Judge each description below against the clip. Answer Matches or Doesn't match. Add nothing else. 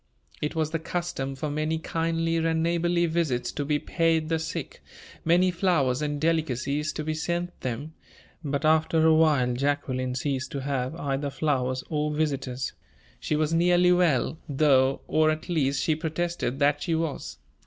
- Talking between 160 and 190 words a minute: Matches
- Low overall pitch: Doesn't match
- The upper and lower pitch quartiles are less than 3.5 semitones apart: Matches